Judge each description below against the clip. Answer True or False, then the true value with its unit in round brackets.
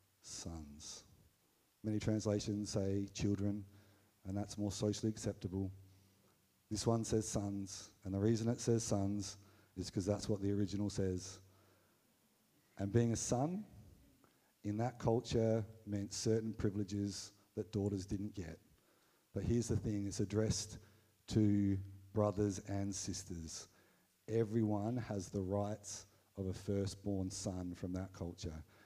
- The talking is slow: True (130 wpm)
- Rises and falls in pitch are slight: True (1.8 semitones)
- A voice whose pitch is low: True (100 Hz)